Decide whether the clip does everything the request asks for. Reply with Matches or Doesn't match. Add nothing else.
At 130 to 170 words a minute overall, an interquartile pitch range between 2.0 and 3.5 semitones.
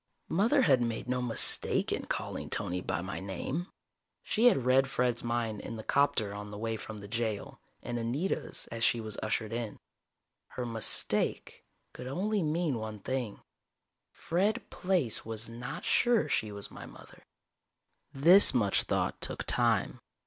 Doesn't match